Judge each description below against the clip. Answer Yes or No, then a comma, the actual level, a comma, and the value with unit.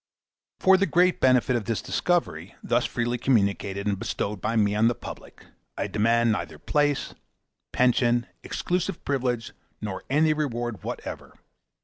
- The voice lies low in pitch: Yes, low, 120 Hz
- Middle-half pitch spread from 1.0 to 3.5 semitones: No, average, 5.1 semitones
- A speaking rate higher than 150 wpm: No, average, 145 wpm